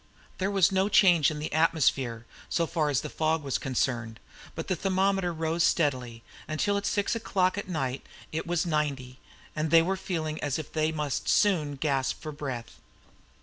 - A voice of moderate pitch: Yes, medium, 155 Hz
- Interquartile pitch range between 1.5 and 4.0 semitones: No, average, 4.4 semitones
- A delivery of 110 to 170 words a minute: No, average, 185 wpm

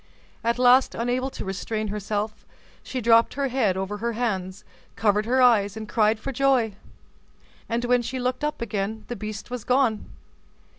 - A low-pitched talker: No, high, 230 Hz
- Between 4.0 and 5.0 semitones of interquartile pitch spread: No, average, 2.9 semitones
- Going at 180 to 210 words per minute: No, average, 165 wpm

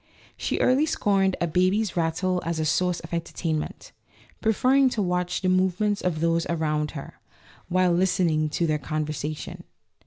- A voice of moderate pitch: Yes, medium, 175 Hz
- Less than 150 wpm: No, average, 155 wpm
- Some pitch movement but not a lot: Yes, average, 3.1 semitones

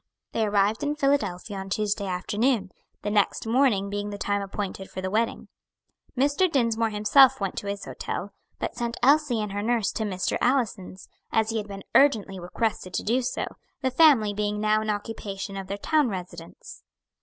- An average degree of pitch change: Yes, average, 3.4 semitones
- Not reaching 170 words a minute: No, average, 180 wpm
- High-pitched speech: Yes, high, 210 Hz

